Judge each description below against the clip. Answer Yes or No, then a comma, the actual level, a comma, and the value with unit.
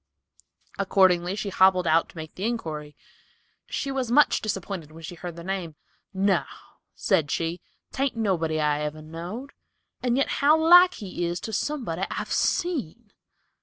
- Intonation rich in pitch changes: Yes, wide, 6.3 semitones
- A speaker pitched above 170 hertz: Yes, high, 190 Hz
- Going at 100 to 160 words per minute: Yes, average, 155 wpm